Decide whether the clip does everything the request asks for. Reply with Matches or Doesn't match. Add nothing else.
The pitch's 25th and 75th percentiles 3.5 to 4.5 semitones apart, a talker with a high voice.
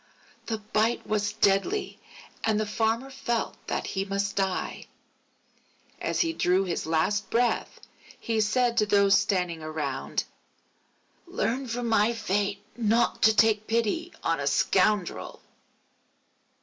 Doesn't match